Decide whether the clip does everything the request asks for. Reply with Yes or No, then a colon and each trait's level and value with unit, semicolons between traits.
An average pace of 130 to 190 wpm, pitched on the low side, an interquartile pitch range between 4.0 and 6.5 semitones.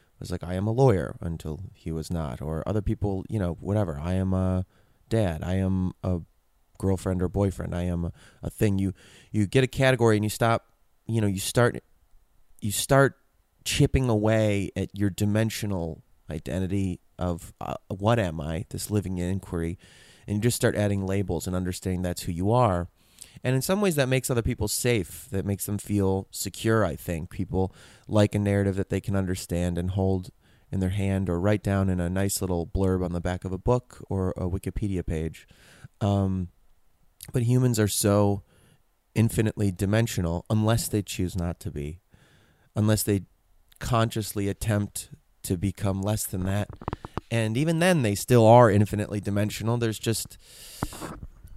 No: average, 175 wpm; low, 100 Hz; average, 3.3 semitones